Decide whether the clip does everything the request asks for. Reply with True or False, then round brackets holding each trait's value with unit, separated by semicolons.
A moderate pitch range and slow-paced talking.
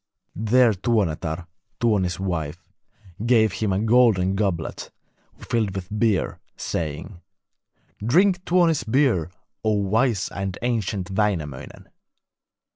True (4.3 semitones; 100 wpm)